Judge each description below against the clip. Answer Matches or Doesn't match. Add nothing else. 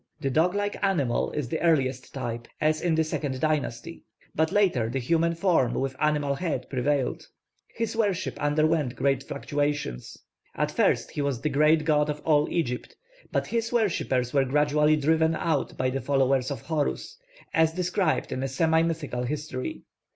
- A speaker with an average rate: Matches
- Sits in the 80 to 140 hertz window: Doesn't match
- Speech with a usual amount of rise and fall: Matches